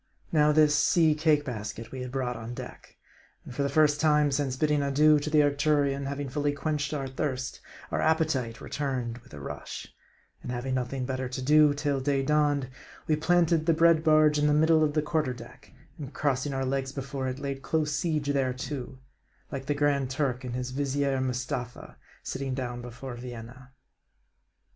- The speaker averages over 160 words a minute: Yes, average, 180 wpm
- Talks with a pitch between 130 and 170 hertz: Yes, medium, 140 Hz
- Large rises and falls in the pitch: No, average, 2.7 semitones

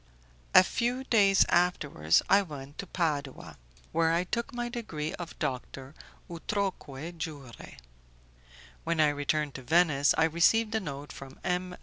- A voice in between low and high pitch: Yes, medium, 165 Hz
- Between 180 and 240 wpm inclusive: No, average, 140 wpm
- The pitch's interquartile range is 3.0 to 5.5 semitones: Yes, average, 5.1 semitones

